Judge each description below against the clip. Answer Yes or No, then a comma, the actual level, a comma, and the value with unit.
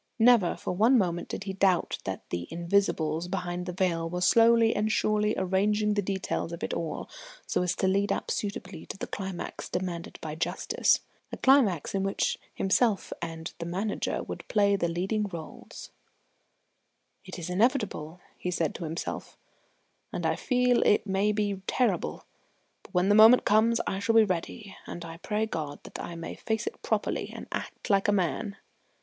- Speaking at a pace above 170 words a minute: Yes, average, 180 wpm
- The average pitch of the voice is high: Yes, high, 195 Hz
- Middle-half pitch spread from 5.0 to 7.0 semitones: No, average, 3.5 semitones